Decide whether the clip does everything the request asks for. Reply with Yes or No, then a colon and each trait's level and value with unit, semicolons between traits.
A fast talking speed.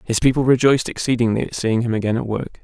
Yes: fast, 230 wpm